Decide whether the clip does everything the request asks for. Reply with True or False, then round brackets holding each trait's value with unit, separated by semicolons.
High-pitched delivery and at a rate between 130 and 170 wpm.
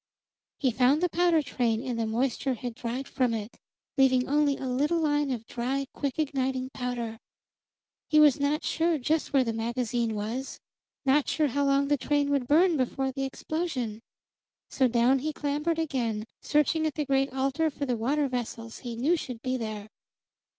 False (265 Hz; 180 wpm)